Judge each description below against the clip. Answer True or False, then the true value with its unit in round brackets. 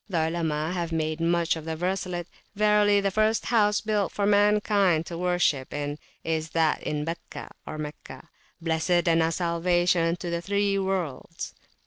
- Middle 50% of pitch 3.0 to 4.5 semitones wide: True (3.4 semitones)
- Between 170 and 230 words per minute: False (155 wpm)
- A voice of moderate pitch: True (170 Hz)